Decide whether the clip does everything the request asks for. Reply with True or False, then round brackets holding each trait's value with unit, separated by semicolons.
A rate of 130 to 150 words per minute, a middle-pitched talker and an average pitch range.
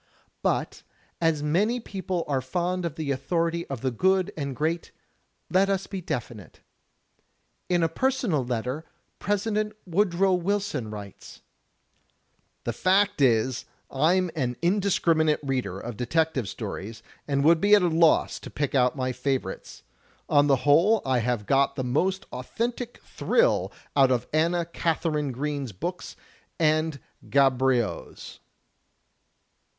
False (135 wpm; 155 Hz; 5.9 semitones)